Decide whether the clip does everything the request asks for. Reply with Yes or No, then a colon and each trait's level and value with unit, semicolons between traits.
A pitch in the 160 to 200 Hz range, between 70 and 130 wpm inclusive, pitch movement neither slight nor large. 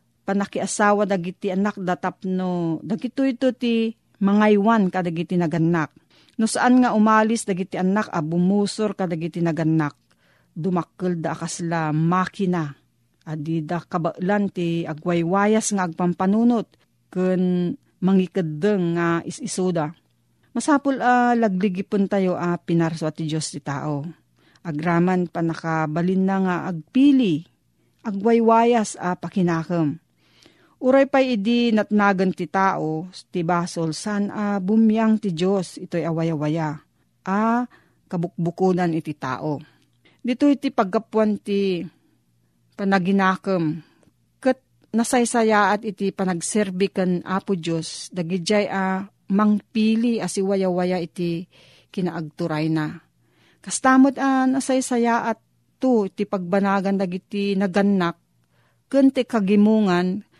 Yes: medium, 185 Hz; slow, 110 wpm; average, 4.0 semitones